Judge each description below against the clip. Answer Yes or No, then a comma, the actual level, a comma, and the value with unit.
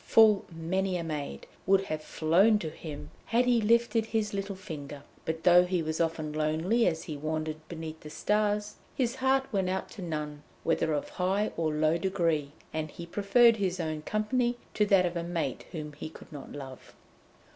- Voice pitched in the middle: Yes, medium, 175 Hz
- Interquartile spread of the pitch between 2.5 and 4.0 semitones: No, average, 4.9 semitones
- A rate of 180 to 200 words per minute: Yes, average, 190 wpm